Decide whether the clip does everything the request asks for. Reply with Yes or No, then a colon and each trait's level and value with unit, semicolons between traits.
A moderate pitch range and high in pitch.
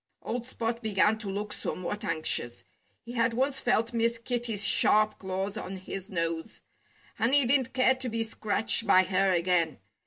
Yes: average, 3.7 semitones; high, 215 Hz